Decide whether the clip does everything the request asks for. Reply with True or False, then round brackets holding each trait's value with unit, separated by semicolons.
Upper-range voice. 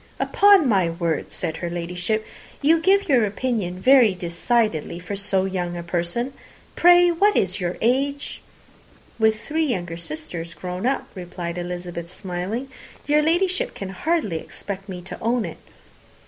True (195 Hz)